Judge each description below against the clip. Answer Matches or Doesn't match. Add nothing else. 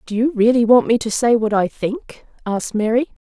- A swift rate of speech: Matches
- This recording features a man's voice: Doesn't match